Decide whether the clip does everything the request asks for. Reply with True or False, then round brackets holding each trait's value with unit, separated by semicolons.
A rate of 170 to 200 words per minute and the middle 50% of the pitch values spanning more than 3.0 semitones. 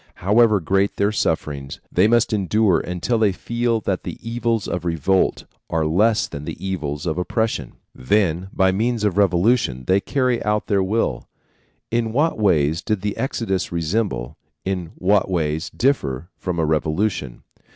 False (160 wpm; 5.0 semitones)